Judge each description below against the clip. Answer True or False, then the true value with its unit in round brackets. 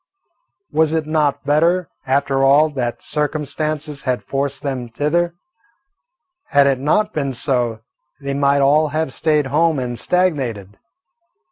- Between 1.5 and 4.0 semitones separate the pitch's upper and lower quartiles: True (2.4 semitones)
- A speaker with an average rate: False (130 wpm)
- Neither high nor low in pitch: True (145 Hz)